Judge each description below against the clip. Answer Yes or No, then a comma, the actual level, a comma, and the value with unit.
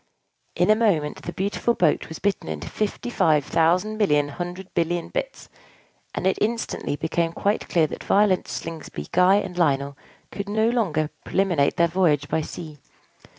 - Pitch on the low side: No, medium, 175 Hz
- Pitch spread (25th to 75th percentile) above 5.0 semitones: No, average, 4.6 semitones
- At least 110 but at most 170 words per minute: Yes, average, 160 wpm